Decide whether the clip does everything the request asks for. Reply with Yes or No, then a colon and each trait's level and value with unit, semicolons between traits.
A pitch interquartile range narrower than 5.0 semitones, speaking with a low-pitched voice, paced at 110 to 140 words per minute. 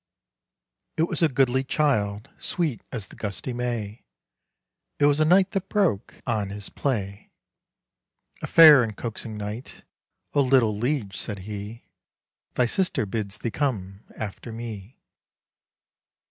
No: average, 5.3 semitones; low, 115 Hz; slow, 135 wpm